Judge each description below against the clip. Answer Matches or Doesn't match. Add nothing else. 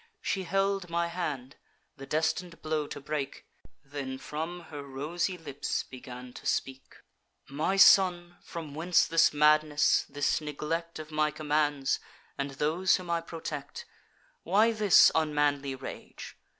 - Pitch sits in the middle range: Matches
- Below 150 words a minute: Matches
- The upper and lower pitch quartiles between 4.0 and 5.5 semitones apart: Doesn't match